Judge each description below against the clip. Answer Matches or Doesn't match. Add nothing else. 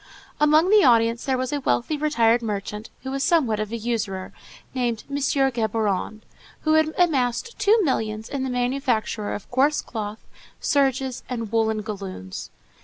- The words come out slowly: Doesn't match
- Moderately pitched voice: Doesn't match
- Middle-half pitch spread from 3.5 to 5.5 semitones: Matches